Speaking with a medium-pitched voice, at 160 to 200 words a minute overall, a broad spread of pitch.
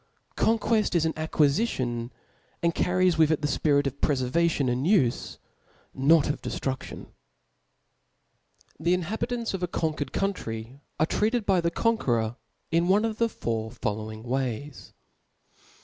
No: medium, 155 Hz; slow, 135 wpm; wide, 6.3 semitones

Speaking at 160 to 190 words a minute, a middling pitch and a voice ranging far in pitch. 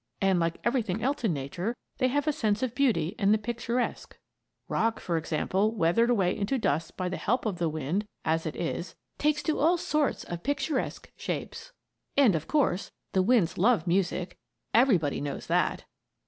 No: average, 175 wpm; high, 205 Hz; wide, 6.3 semitones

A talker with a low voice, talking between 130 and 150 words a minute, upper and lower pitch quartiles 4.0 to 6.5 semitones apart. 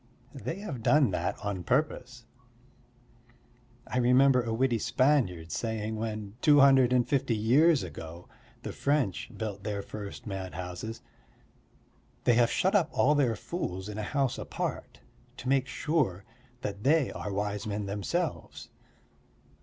Yes: low, 115 Hz; average, 140 wpm; average, 5.2 semitones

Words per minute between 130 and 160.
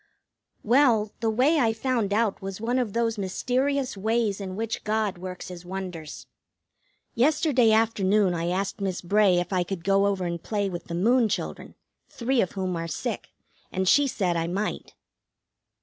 No: average, 170 wpm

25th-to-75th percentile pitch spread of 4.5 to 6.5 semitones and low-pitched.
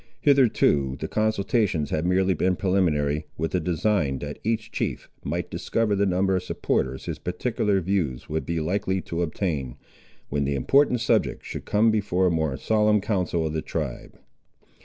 Yes: average, 5.1 semitones; very low, 90 Hz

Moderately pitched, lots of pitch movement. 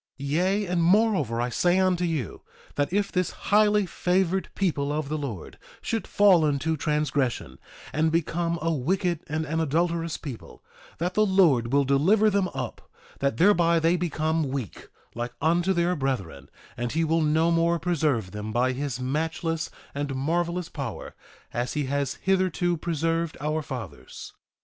No: medium, 160 Hz; average, 4.0 semitones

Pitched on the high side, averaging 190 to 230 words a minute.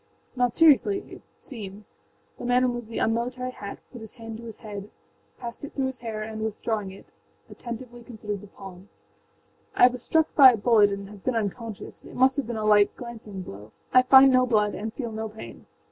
Yes: high, 225 Hz; average, 200 wpm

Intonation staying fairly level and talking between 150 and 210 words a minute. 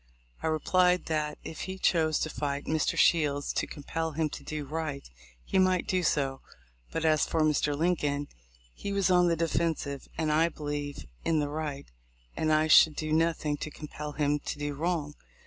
Yes: narrow, 1.9 semitones; average, 180 wpm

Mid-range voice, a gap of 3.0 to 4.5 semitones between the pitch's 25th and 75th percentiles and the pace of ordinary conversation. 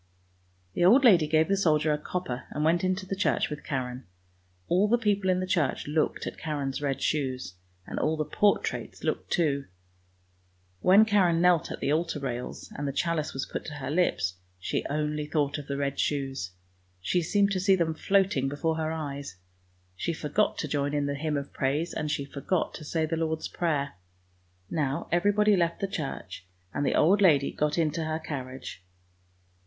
Yes: medium, 155 Hz; average, 3.9 semitones; average, 190 wpm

